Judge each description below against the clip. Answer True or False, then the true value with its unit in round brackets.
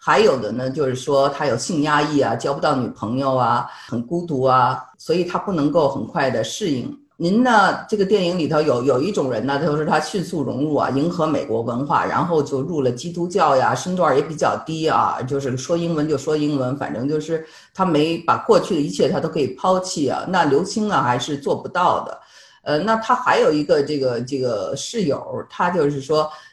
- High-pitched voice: False (150 Hz)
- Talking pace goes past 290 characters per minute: True (305 characters per minute)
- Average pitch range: True (4.0 semitones)